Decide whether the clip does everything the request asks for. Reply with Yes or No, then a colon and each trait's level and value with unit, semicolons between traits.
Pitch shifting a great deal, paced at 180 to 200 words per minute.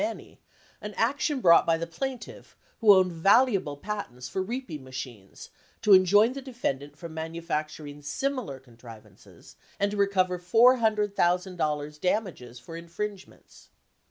No: wide, 5.9 semitones; average, 145 wpm